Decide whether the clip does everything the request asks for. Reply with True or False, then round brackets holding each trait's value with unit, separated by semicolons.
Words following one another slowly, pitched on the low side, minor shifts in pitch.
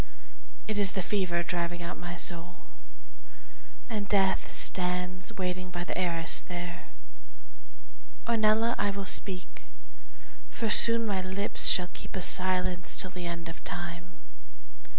False (130 wpm; 180 Hz; 2.3 semitones)